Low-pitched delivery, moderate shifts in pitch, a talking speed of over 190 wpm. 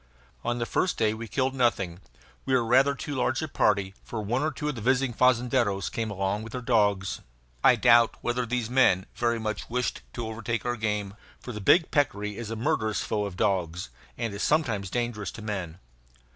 Yes: low, 115 Hz; average, 3.2 semitones; average, 200 wpm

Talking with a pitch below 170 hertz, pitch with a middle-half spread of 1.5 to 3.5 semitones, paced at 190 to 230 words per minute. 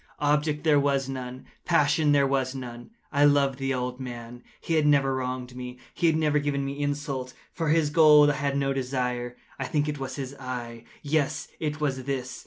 Yes: medium, 140 Hz; narrow, 2.4 semitones; average, 195 wpm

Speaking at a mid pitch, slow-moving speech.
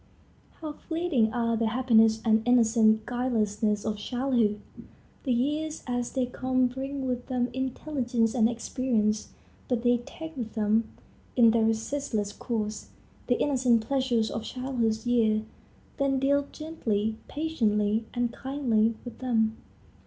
No: high, 240 Hz; slow, 130 wpm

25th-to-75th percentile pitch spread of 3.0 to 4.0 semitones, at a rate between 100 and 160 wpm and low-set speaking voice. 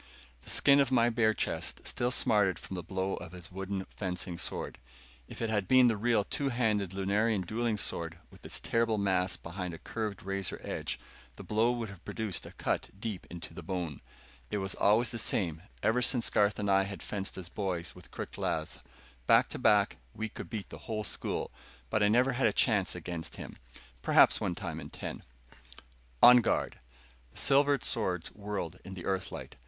No: average, 3.7 semitones; average, 195 wpm; low, 100 Hz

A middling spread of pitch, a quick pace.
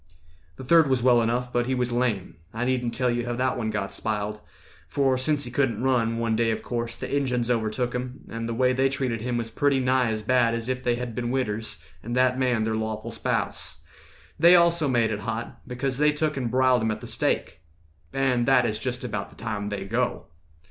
No: narrow, 2.2 semitones; fast, 225 wpm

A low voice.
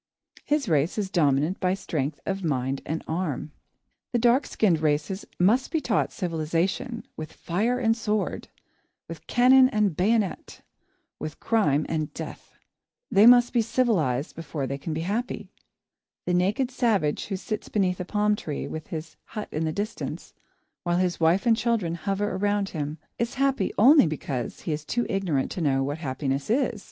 No: medium, 185 Hz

